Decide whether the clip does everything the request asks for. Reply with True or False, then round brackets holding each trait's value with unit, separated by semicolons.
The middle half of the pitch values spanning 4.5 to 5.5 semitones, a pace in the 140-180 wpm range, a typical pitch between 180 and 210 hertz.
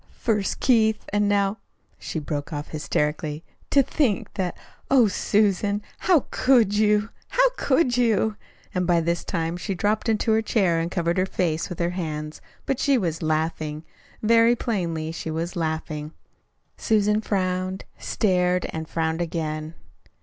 True (5.0 semitones; 150 wpm; 185 Hz)